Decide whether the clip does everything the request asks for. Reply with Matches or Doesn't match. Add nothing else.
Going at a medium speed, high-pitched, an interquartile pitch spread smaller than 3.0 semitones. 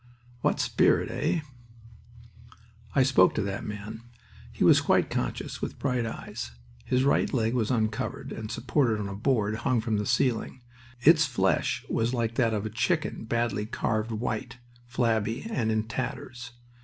Doesn't match